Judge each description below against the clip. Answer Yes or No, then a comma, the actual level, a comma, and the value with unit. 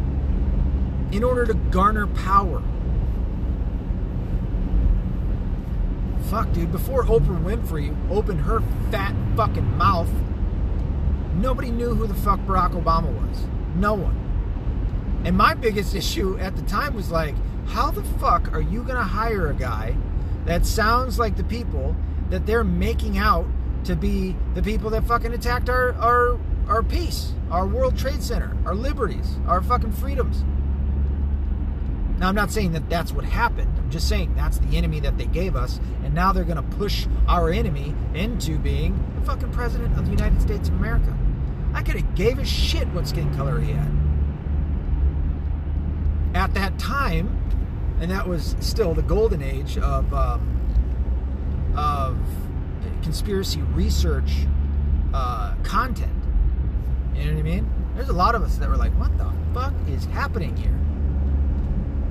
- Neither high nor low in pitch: No, very low, 70 Hz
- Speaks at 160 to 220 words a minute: No, average, 150 wpm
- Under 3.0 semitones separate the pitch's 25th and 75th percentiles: Yes, narrow, 2.5 semitones